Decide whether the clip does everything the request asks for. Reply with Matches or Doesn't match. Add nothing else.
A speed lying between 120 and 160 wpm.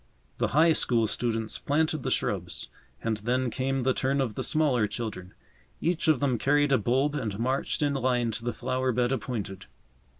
Doesn't match